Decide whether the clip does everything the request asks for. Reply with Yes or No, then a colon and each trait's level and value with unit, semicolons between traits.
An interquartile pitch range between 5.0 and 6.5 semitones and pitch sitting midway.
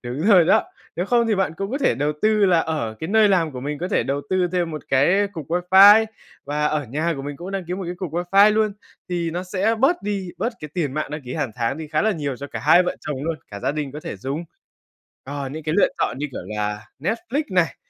Yes: average, 5.3 semitones; medium, 165 Hz